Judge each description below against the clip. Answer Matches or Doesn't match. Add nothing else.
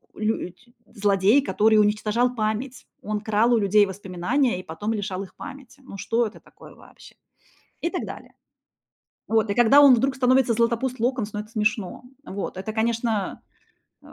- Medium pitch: Doesn't match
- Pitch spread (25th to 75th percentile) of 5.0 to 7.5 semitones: Doesn't match